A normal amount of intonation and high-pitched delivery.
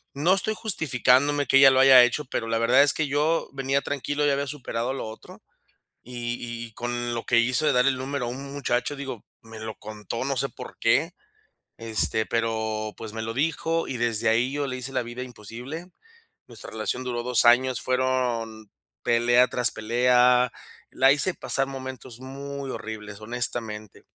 No: average, 3.0 semitones; low, 125 Hz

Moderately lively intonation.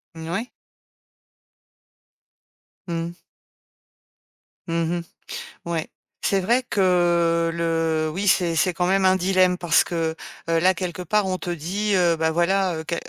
No: narrow, 2.1 semitones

